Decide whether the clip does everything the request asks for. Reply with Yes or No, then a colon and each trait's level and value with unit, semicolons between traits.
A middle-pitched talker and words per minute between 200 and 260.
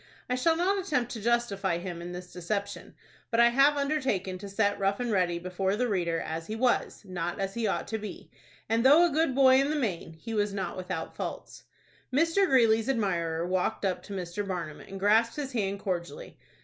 No: high, 205 Hz; fast, 205 wpm